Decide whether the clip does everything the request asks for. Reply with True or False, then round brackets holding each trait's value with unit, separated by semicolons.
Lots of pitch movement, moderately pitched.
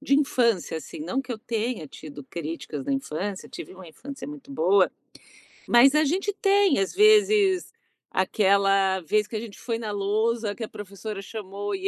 False (6.1 semitones; 215 Hz)